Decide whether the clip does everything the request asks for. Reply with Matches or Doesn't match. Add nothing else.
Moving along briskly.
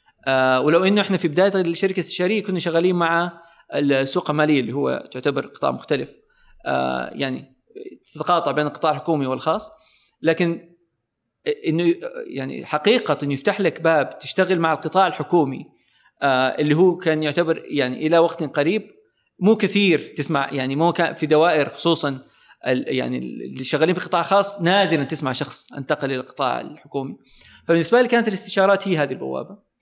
Matches